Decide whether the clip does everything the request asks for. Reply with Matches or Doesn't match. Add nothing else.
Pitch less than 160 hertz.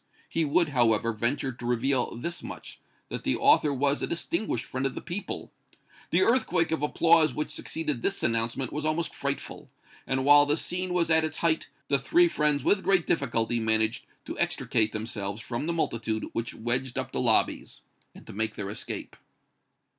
Matches